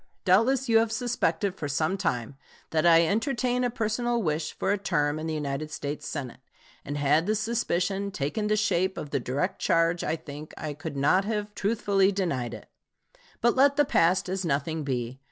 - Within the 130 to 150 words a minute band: No, average, 190 wpm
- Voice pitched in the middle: Yes, medium, 175 Hz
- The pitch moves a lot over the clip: Yes, wide, 6.2 semitones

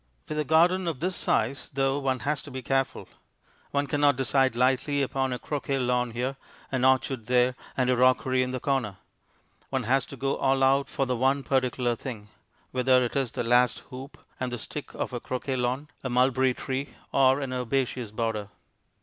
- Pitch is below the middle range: Yes, low, 130 Hz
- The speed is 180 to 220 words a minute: Yes, average, 190 wpm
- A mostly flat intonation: Yes, narrow, 1.6 semitones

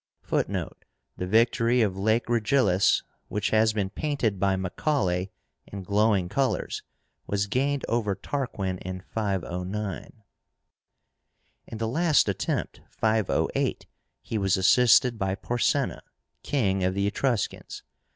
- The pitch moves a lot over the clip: No, average, 3.7 semitones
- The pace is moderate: No, slow, 115 wpm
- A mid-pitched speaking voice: No, low, 105 Hz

